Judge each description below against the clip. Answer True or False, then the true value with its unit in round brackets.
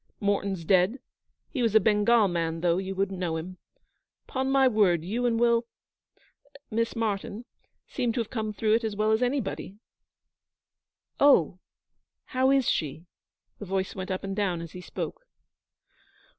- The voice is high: True (205 Hz)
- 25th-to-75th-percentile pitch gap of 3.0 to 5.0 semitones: True (4.0 semitones)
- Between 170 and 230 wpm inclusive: False (155 wpm)